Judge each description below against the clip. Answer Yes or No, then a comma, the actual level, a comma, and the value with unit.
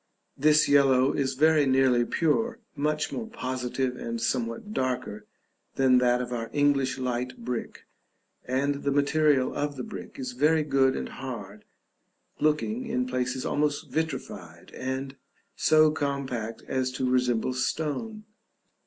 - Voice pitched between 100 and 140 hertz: Yes, low, 135 Hz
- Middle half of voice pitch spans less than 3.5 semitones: Yes, average, 3.1 semitones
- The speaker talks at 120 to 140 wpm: Yes, slow, 135 wpm